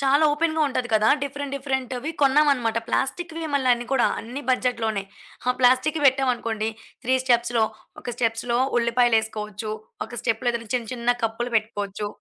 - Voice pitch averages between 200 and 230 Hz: No, high, 245 Hz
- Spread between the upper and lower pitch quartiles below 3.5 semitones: Yes, average, 2.9 semitones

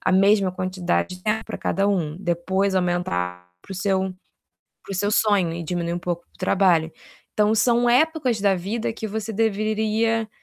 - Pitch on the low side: No, high, 195 Hz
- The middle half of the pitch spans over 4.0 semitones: No, average, 3.6 semitones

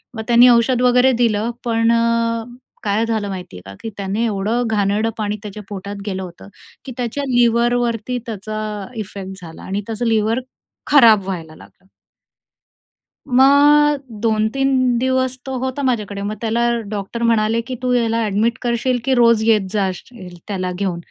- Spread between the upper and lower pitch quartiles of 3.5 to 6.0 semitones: No, average, 3.1 semitones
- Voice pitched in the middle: No, high, 225 Hz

